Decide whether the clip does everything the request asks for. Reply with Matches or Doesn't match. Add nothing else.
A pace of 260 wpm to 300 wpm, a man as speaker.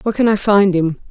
Doesn't match